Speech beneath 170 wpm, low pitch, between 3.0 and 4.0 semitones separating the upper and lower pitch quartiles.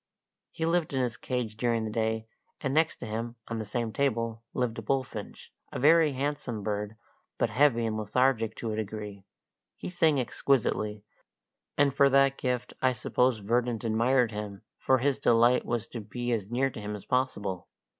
No: average, 175 wpm; low, 120 Hz; average, 3.4 semitones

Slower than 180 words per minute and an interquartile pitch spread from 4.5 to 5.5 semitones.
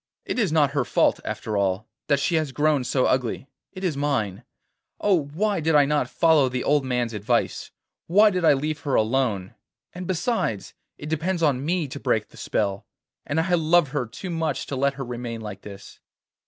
No: average, 195 wpm; average, 4.9 semitones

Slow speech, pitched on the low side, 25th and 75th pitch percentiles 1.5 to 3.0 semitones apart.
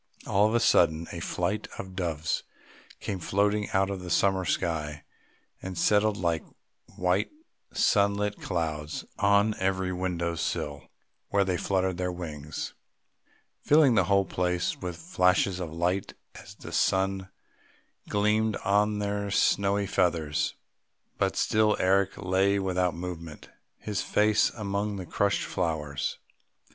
Yes: slow, 130 wpm; very low, 95 Hz; average, 2.7 semitones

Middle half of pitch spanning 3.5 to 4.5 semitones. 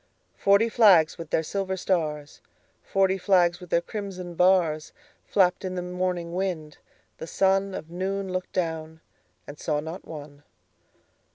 No: average, 3.0 semitones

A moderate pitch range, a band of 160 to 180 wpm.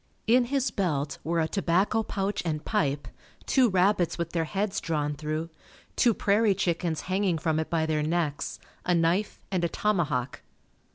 Yes: average, 4.0 semitones; average, 165 wpm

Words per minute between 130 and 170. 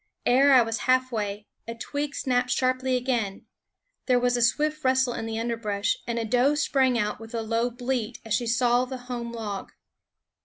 No: average, 185 wpm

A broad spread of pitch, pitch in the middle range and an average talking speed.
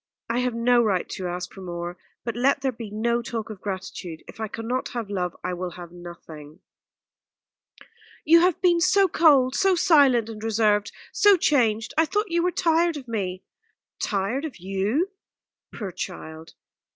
No: wide, 7.1 semitones; high, 225 Hz; average, 170 wpm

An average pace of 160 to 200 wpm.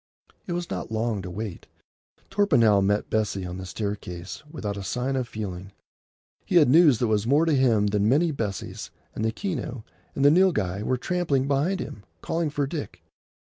Yes: average, 180 wpm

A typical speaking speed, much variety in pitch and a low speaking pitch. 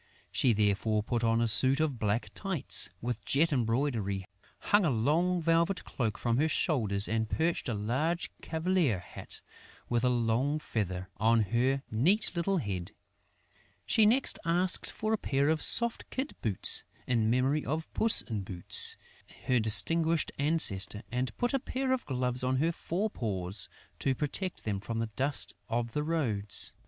Yes: average, 165 wpm; wide, 6.9 semitones; low, 130 Hz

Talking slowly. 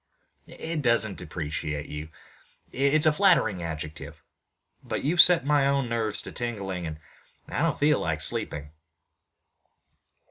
Yes: slow, 130 wpm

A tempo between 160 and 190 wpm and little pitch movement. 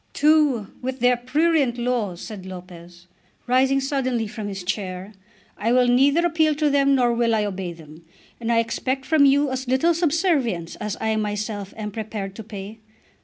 No: average, 175 wpm; average, 5.0 semitones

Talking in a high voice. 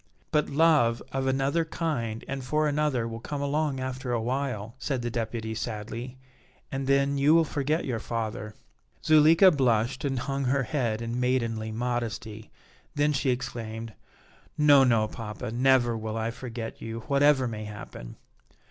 No: low, 125 Hz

